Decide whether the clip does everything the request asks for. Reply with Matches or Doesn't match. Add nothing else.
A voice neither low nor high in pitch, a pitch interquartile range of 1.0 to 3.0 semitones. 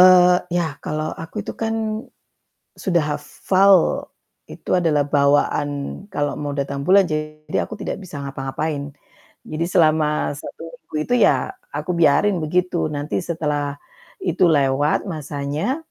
Doesn't match